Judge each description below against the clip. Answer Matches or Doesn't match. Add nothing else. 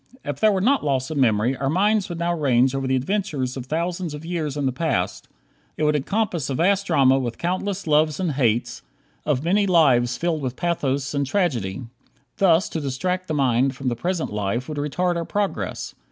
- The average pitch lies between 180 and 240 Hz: Doesn't match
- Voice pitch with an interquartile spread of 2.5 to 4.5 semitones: Doesn't match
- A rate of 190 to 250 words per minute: Matches